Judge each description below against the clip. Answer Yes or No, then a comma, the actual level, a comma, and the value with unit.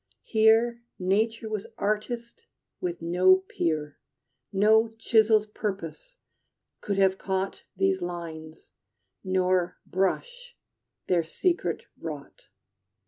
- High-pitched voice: Yes, high, 195 Hz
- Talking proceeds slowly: Yes, slow, 90 wpm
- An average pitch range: Yes, average, 3.6 semitones